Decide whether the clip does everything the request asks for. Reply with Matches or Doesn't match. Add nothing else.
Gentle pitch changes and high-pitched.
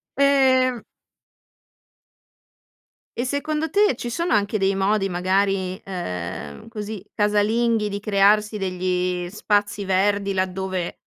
Doesn't match